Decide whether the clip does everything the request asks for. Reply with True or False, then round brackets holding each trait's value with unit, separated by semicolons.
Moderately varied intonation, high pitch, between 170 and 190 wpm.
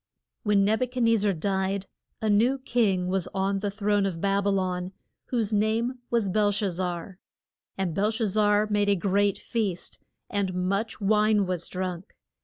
False (2.2 semitones; 200 Hz; 180 wpm)